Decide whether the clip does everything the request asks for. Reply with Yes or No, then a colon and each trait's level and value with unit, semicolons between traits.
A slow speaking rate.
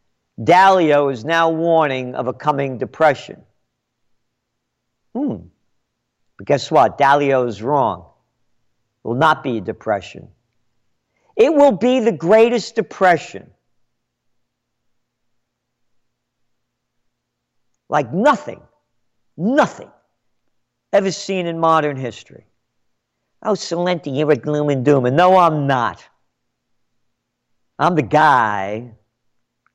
Yes: slow, 100 wpm